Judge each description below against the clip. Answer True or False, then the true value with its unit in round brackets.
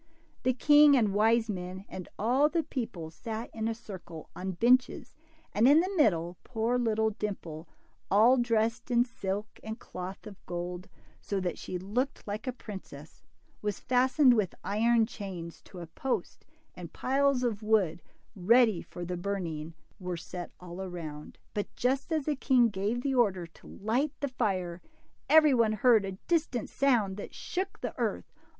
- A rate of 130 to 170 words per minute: True (165 wpm)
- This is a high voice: True (215 Hz)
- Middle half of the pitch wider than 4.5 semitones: True (5.2 semitones)